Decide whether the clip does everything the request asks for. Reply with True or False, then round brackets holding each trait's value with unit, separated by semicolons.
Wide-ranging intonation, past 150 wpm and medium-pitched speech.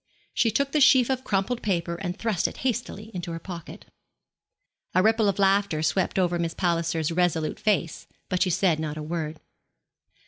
False (4.2 semitones; 175 wpm; 180 Hz)